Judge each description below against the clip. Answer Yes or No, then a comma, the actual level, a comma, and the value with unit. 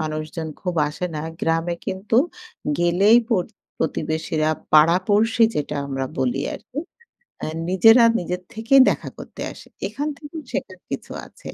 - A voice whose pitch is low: No, medium, 175 Hz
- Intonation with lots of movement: Yes, wide, 5.9 semitones